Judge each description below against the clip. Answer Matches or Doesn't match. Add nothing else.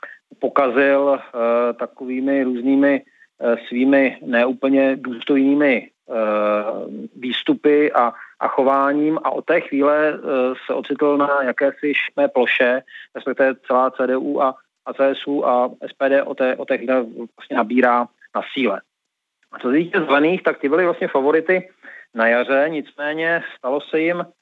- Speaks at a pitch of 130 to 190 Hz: Matches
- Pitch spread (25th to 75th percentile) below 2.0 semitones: Doesn't match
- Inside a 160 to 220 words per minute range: Doesn't match